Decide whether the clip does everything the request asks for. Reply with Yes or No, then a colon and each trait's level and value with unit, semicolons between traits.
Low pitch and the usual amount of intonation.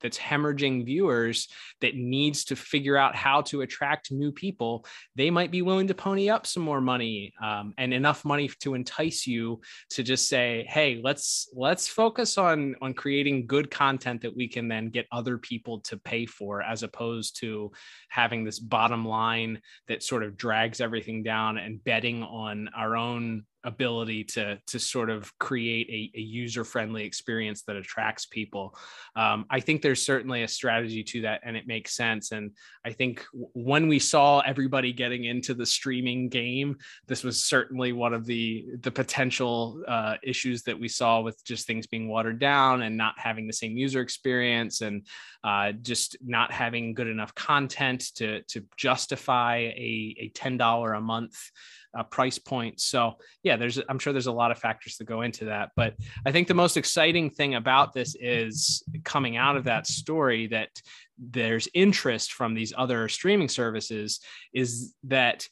Yes: low, 120 Hz; average, 3.2 semitones